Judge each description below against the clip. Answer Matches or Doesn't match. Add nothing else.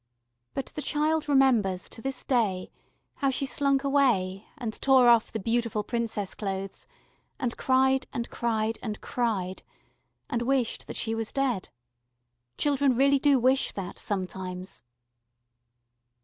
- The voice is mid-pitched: Doesn't match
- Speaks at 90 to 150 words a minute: Matches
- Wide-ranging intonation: Doesn't match